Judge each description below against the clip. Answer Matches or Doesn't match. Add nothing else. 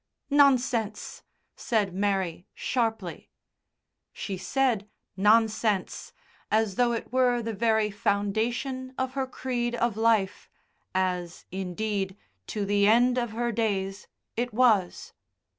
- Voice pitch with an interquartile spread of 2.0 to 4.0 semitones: Matches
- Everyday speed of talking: Doesn't match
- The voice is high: Matches